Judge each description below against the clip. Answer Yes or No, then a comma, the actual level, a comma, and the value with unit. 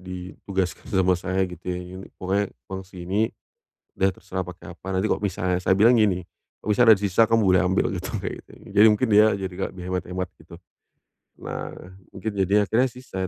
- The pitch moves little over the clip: Yes, narrow, 2.1 semitones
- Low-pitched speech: Yes, very low, 95 Hz